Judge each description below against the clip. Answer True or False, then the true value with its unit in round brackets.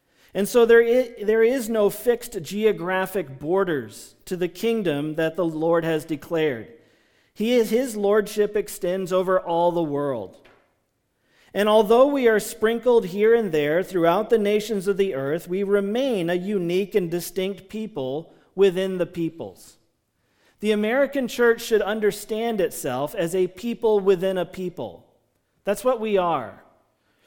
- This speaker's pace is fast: False (140 wpm)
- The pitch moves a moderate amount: True (4.0 semitones)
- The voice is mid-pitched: False (200 Hz)